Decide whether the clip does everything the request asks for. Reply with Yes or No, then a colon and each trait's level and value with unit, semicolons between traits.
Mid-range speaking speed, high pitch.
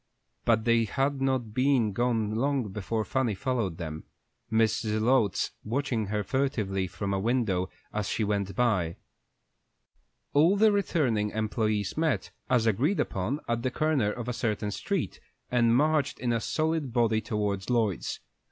No: average, 150 wpm; low, 115 Hz